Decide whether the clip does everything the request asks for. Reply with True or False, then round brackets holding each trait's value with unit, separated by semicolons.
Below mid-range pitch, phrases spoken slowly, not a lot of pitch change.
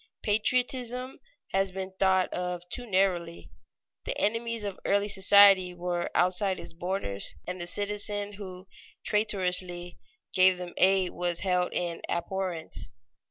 False (190 Hz; 125 wpm; 2.3 semitones)